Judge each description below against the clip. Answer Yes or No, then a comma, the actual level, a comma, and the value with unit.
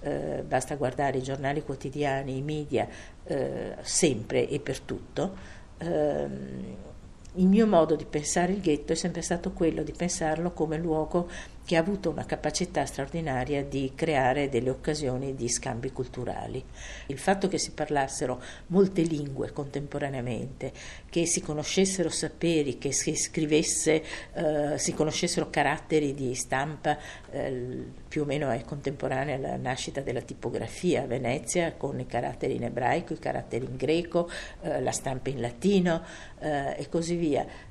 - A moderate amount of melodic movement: Yes, average, 3.6 semitones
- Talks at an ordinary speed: Yes, average, 150 wpm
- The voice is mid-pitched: Yes, medium, 150 Hz